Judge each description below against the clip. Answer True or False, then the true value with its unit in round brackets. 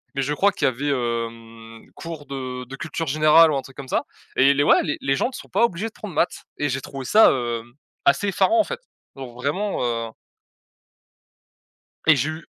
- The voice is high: False (140 Hz)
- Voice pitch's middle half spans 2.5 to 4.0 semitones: False (4.4 semitones)